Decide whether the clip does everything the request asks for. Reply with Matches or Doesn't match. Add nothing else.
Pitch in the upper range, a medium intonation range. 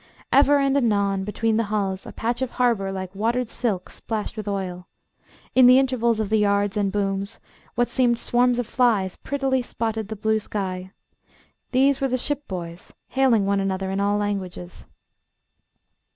Matches